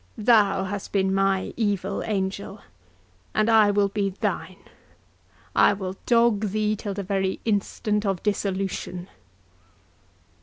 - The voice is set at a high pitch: Yes, high, 200 Hz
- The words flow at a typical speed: No, slow, 115 wpm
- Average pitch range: No, narrow, 1.6 semitones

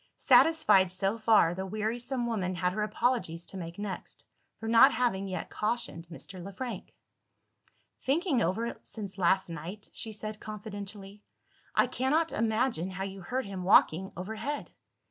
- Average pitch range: Yes, average, 3.9 semitones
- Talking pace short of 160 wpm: Yes, average, 150 wpm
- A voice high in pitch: Yes, high, 205 Hz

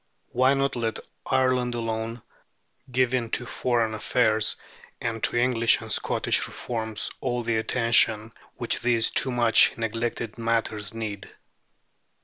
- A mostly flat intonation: Yes, narrow, 1.6 semitones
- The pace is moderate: No, slow, 125 wpm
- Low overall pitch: Yes, low, 115 Hz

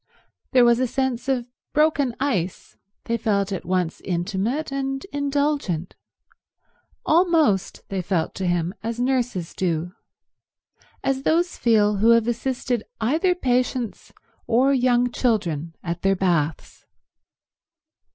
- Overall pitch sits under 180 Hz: No, high, 235 Hz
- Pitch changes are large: Yes, wide, 6.1 semitones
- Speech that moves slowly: Yes, slow, 115 wpm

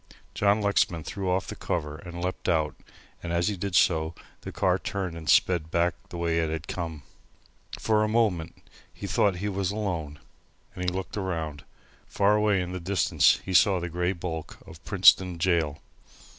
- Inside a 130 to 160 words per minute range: No, average, 180 wpm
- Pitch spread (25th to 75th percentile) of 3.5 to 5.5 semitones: No, average, 2.9 semitones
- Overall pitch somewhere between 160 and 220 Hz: No, very low, 90 Hz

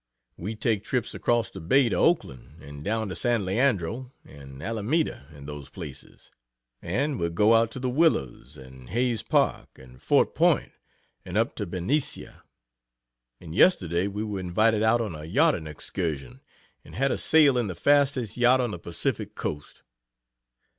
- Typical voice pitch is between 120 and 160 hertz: No, low, 105 Hz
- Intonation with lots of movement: Yes, wide, 7.3 semitones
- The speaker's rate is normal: Yes, average, 165 wpm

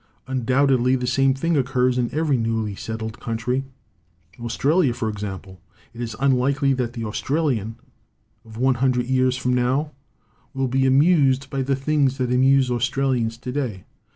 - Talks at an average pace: Yes, average, 155 wpm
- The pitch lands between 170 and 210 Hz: No, low, 130 Hz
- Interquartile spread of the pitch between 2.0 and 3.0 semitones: Yes, narrow, 2.4 semitones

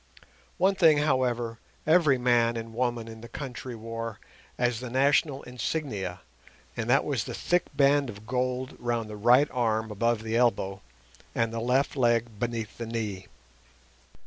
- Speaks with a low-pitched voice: Yes, low, 120 Hz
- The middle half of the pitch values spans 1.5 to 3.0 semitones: Yes, narrow, 2.5 semitones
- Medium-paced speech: Yes, average, 155 wpm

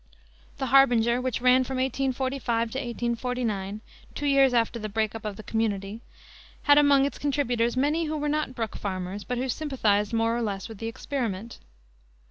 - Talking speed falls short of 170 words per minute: No, average, 175 wpm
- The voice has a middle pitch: No, high, 240 Hz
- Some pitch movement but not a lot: Yes, average, 3.4 semitones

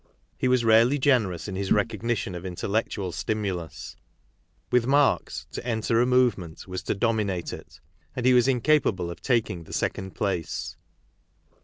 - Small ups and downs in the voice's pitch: No, average, 4.9 semitones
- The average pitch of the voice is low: Yes, low, 110 Hz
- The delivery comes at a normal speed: Yes, average, 150 wpm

